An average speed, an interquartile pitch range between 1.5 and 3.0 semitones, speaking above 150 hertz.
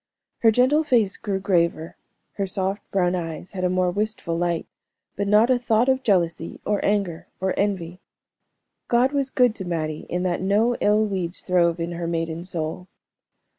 No: average, 170 wpm; average, 3.8 semitones; high, 190 Hz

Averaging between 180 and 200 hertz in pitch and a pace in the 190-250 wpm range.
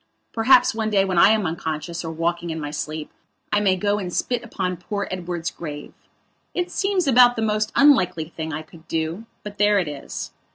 Yes: medium, 185 Hz; average, 200 wpm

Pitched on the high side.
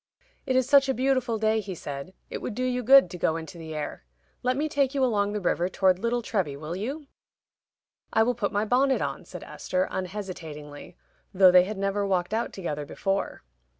Yes: high, 205 Hz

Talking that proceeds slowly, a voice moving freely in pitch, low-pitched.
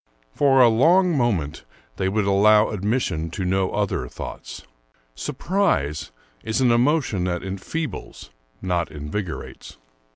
Yes: slow, 125 wpm; wide, 6.4 semitones; low, 105 Hz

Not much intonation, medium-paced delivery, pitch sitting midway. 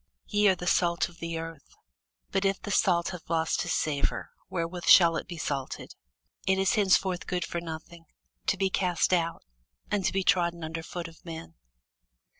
Yes: narrow, 2.2 semitones; average, 190 wpm; medium, 170 Hz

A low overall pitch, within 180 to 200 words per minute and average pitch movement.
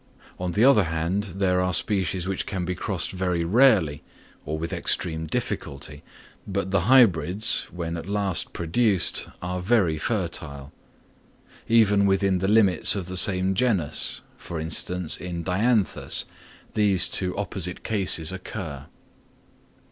No: very low, 90 Hz; slow, 135 wpm; average, 3.1 semitones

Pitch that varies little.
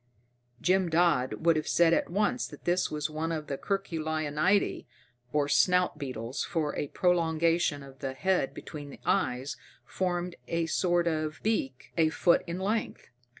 No: average, 3.2 semitones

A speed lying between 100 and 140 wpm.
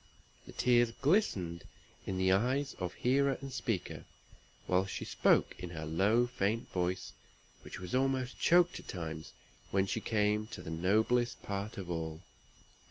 No: average, 155 wpm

